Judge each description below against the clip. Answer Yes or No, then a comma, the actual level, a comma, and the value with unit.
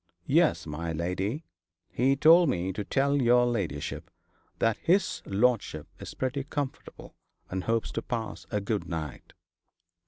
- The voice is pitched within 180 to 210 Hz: No, low, 115 Hz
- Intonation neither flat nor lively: No, wide, 6.6 semitones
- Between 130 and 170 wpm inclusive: Yes, slow, 135 wpm